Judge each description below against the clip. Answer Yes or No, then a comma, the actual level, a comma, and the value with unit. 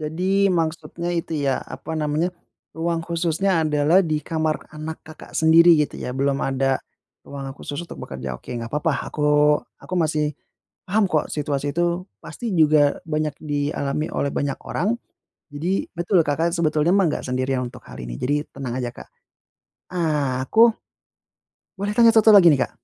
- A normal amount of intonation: Yes, average, 3.1 semitones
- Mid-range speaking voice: Yes, medium, 155 Hz